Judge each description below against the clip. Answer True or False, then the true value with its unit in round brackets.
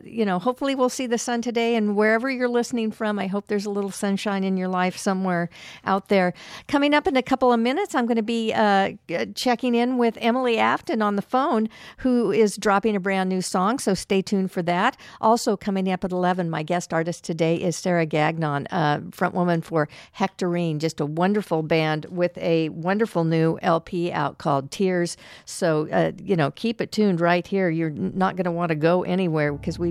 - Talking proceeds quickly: True (215 wpm)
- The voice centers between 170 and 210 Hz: True (190 Hz)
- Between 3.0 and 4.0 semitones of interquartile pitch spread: False (4.4 semitones)